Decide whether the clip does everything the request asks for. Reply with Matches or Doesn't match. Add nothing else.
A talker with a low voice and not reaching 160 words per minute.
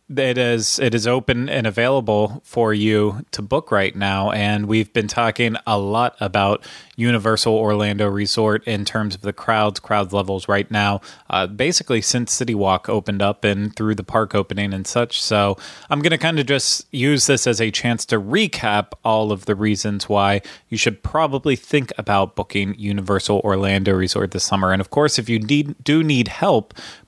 Doesn't match